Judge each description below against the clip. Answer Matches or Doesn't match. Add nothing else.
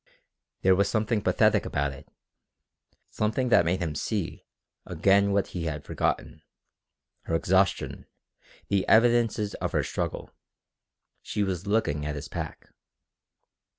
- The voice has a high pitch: Doesn't match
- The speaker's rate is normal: Doesn't match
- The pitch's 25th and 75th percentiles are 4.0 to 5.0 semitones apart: Matches